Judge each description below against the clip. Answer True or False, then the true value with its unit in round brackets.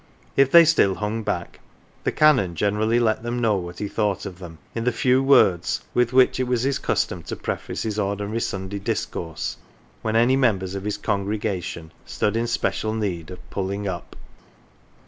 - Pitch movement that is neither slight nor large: True (3.8 semitones)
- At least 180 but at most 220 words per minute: True (185 wpm)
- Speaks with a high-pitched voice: False (105 Hz)